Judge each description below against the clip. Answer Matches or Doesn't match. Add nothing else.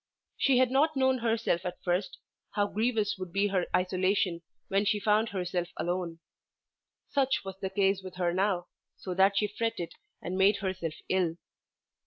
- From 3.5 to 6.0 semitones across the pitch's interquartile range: Doesn't match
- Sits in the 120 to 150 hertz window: Doesn't match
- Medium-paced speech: Matches